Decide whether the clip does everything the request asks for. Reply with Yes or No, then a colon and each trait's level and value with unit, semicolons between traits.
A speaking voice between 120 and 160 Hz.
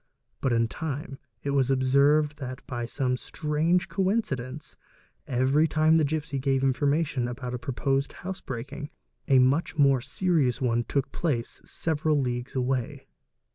Yes: medium, 140 Hz